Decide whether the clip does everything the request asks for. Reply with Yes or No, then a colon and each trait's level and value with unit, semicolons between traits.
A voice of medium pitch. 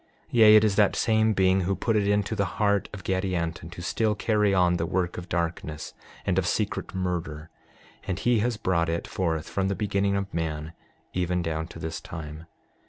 No: very low, 95 Hz